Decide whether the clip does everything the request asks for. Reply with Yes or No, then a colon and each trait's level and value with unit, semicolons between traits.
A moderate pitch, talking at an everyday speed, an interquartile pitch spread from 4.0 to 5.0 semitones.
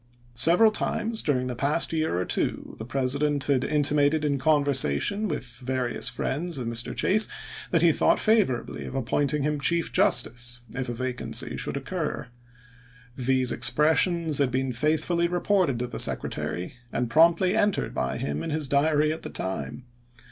Yes: medium, 145 Hz; average, 160 wpm; average, 4.3 semitones